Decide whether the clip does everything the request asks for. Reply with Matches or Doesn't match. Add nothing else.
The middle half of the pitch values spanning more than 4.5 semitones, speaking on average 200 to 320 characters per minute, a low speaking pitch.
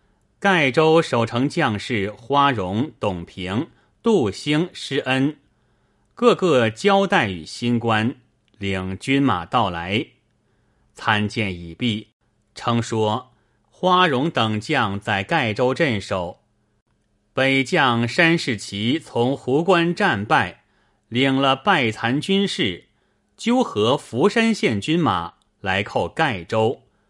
Doesn't match